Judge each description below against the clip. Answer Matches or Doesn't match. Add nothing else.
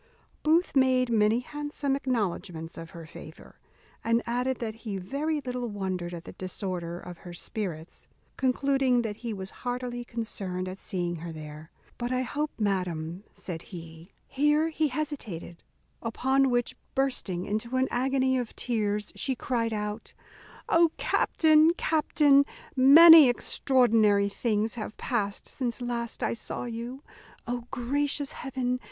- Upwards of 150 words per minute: Doesn't match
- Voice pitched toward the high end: Matches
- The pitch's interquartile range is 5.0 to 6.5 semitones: Matches